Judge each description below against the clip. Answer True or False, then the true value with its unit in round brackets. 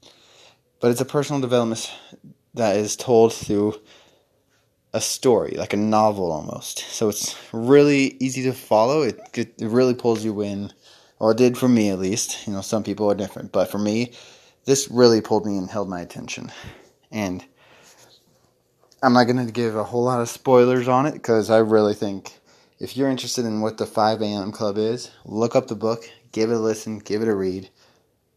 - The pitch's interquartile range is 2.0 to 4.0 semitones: True (2.9 semitones)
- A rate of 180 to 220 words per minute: True (190 wpm)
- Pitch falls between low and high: False (110 Hz)